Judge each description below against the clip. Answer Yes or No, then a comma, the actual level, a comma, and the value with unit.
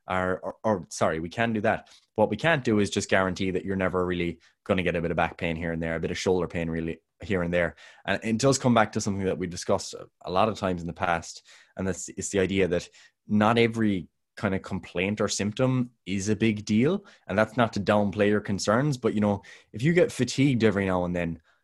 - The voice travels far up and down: No, average, 3.8 semitones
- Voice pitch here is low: Yes, low, 100 Hz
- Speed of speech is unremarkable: No, fast, 250 wpm